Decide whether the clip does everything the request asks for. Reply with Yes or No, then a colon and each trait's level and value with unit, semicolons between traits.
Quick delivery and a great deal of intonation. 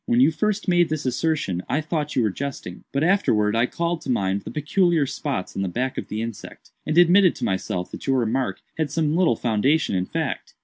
Yes: fast, 220 wpm; wide, 6.7 semitones